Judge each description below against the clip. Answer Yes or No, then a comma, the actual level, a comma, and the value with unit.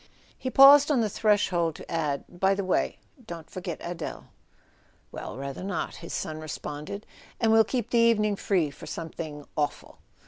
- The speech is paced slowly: No, average, 165 wpm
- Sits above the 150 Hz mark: Yes, medium, 185 Hz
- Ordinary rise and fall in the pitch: No, wide, 5.8 semitones